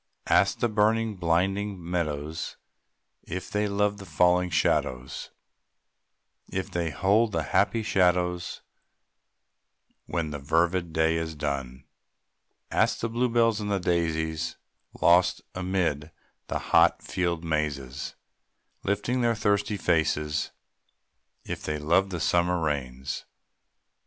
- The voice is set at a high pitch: No, very low, 85 Hz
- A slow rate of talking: Yes, slow, 115 wpm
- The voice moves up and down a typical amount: Yes, average, 4.2 semitones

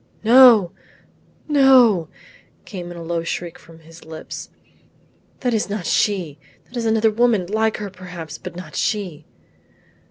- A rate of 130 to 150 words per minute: Yes, average, 140 wpm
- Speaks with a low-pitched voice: No, high, 195 Hz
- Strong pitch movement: No, average, 4.8 semitones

